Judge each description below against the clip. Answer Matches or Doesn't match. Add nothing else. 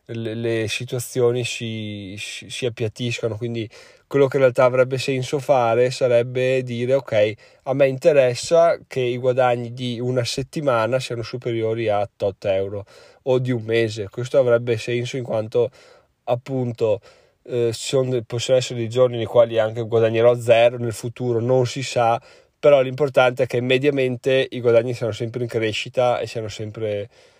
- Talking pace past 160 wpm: Doesn't match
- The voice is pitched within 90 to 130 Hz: Matches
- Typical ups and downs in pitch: Doesn't match